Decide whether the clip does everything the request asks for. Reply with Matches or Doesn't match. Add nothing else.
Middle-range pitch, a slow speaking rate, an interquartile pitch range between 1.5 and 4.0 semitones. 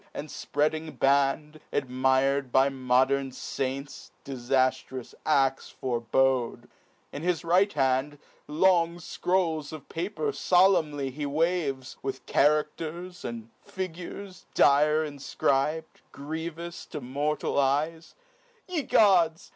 Matches